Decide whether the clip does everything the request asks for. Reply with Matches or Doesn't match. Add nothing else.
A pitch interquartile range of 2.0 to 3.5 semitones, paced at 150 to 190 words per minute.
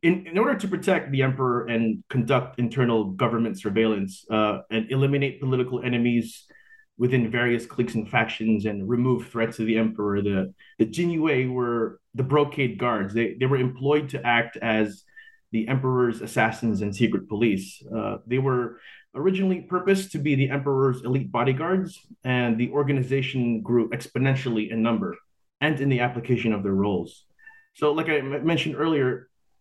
Doesn't match